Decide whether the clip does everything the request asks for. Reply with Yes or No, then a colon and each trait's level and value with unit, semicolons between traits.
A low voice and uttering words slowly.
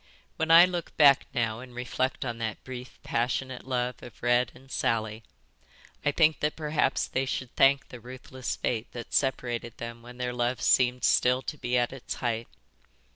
No: low, 125 Hz; average, 180 wpm